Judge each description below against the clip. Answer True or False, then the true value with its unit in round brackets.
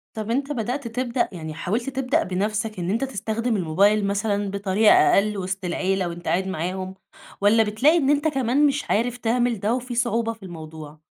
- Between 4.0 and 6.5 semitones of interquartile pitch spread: True (4.4 semitones)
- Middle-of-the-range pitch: False (215 Hz)